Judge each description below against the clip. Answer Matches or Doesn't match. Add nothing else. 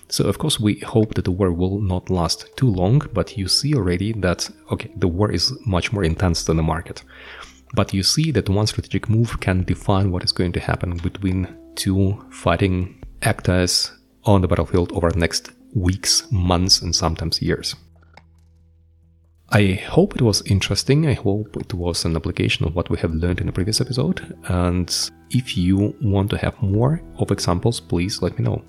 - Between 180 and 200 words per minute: Matches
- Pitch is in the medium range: Doesn't match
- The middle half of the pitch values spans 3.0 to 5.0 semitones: Matches